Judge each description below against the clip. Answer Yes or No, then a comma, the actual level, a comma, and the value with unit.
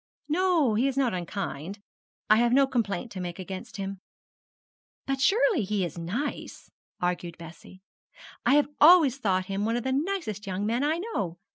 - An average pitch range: No, wide, 6.7 semitones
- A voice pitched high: Yes, high, 220 Hz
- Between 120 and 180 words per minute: Yes, average, 170 wpm